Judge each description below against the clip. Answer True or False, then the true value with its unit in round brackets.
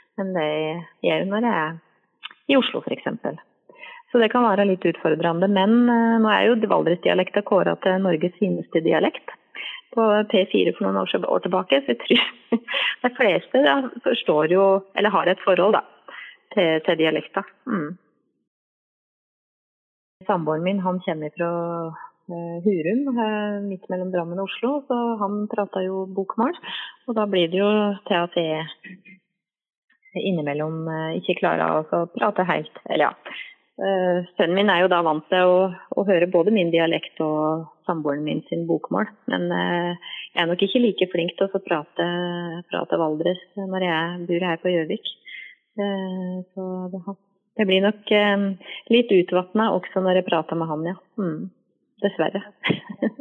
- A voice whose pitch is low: False (185 Hz)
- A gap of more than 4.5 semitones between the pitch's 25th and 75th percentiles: False (3.3 semitones)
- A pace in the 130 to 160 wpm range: True (155 wpm)